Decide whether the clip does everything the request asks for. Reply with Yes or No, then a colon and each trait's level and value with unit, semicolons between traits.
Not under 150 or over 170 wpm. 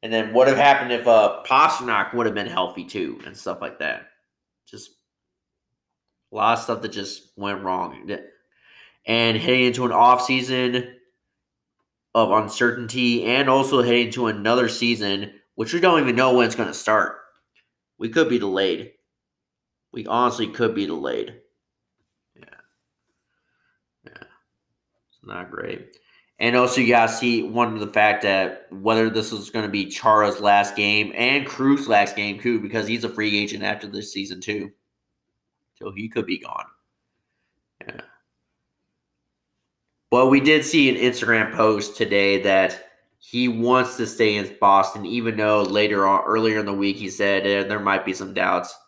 Yes: average, 165 wpm